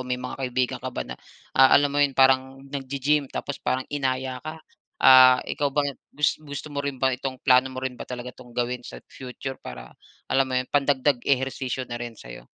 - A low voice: Yes, low, 130 Hz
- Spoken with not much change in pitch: Yes, narrow, 1.6 semitones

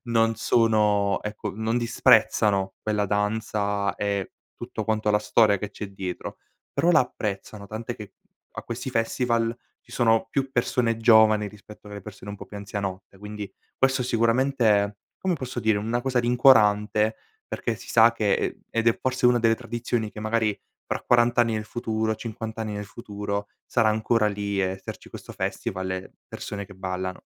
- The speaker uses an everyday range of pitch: No, narrow, 2.3 semitones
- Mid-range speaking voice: No, low, 110 Hz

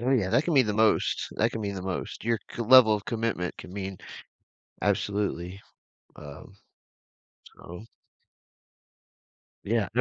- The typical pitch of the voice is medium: No, low, 105 Hz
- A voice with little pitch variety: No, average, 3.3 semitones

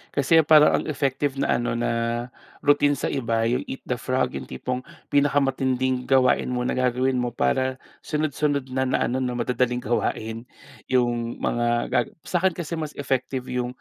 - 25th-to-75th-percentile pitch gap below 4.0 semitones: Yes, narrow, 2.4 semitones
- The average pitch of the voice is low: Yes, low, 130 Hz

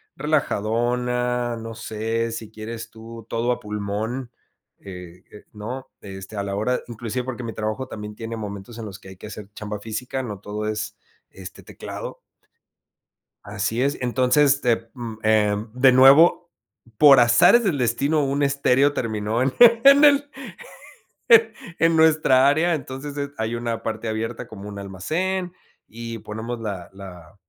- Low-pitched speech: Yes, low, 115 Hz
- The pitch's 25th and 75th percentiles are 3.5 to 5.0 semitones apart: Yes, average, 4.0 semitones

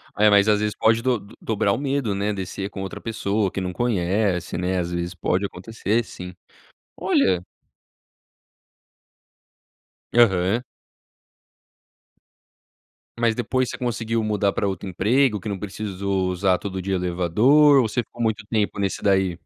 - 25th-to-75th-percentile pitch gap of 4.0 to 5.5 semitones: No, average, 3.3 semitones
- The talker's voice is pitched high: No, low, 100 Hz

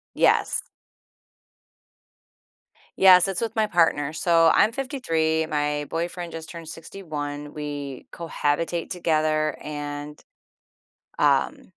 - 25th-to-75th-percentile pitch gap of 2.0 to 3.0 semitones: Yes, average, 2.7 semitones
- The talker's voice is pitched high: No, medium, 160 Hz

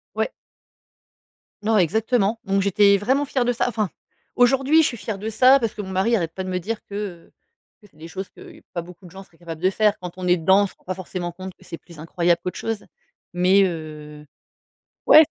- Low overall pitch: No, high, 190 Hz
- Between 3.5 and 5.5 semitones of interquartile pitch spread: Yes, average, 4.0 semitones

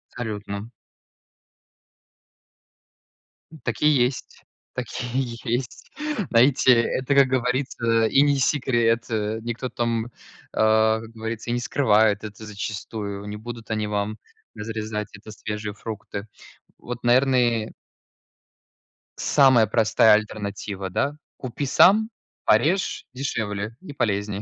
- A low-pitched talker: Yes, low, 115 Hz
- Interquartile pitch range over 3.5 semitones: No, average, 2.9 semitones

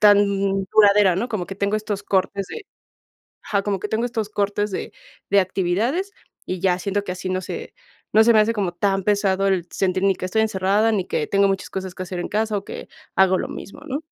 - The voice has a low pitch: No, high, 200 Hz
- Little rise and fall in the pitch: Yes, narrow, 2.2 semitones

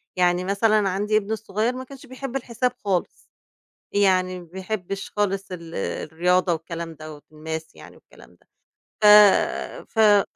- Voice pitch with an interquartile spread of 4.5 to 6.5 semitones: No, average, 3.6 semitones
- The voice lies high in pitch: Yes, high, 195 Hz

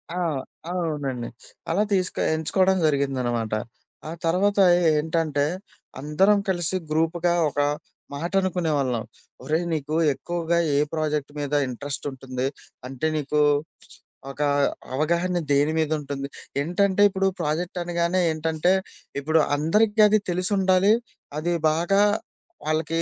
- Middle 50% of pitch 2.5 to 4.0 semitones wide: Yes, average, 3.7 semitones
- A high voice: No, medium, 160 Hz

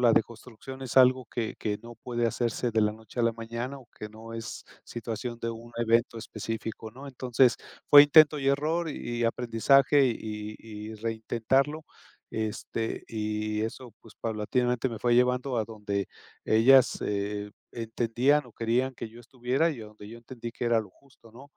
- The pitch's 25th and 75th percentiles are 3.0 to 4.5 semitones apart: No, narrow, 2.4 semitones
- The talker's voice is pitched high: No, low, 115 Hz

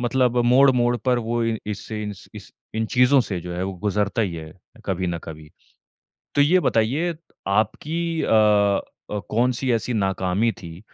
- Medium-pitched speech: No, low, 110 Hz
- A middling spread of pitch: Yes, average, 4.2 semitones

